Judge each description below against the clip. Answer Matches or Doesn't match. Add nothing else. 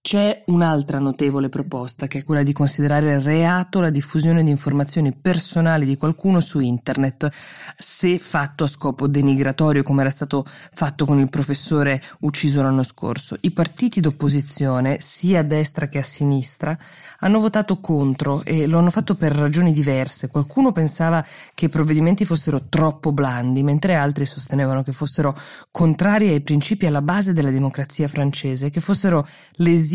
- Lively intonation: Doesn't match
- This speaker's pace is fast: Doesn't match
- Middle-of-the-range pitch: Matches